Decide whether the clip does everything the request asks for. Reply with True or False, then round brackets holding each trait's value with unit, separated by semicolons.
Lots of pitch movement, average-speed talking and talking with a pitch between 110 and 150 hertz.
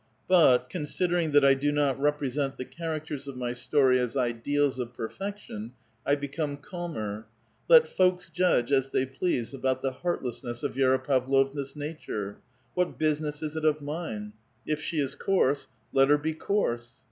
False (3.4 semitones; 160 wpm; 140 Hz)